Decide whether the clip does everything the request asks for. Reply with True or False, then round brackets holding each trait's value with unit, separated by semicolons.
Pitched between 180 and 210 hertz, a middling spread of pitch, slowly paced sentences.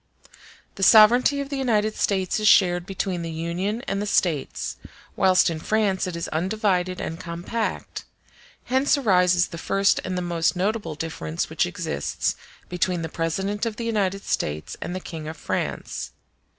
False (185 Hz; 3.9 semitones; 165 wpm)